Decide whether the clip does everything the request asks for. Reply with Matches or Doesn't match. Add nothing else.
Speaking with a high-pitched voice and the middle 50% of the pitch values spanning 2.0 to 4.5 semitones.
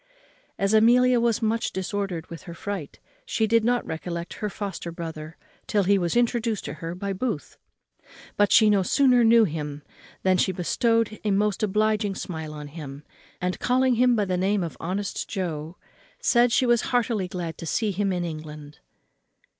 Doesn't match